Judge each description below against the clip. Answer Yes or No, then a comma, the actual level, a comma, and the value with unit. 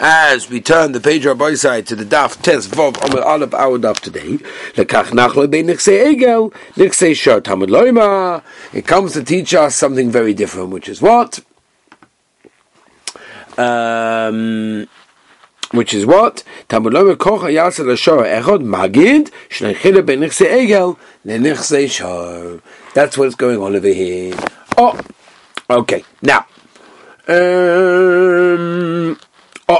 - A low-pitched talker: No, medium, 150 Hz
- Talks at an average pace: No, slow, 125 wpm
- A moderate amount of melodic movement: No, wide, 7.9 semitones